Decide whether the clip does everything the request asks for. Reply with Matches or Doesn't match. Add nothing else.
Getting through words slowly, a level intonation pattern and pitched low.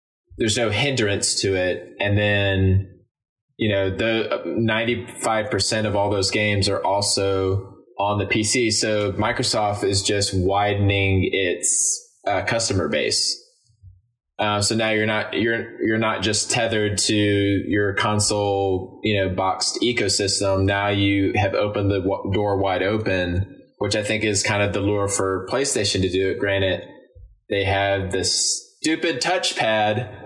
Doesn't match